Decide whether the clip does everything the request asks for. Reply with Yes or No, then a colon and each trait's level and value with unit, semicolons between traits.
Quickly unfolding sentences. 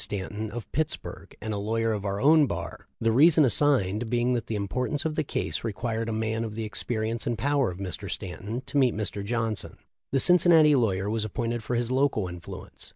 Yes: fast, 215 wpm